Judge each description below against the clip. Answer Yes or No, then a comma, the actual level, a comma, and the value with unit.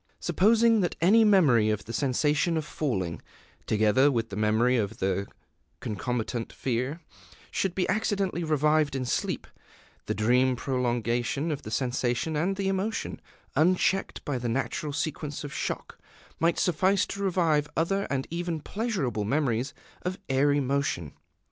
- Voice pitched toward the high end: No, medium, 145 Hz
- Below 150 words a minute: Yes, average, 140 wpm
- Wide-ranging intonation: Yes, wide, 6.4 semitones